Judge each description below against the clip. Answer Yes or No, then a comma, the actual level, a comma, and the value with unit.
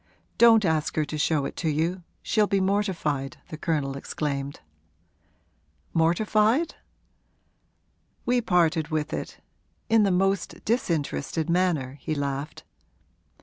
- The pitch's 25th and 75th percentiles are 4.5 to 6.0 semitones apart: Yes, average, 4.9 semitones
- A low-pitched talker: No, medium, 165 Hz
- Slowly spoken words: Yes, slow, 115 wpm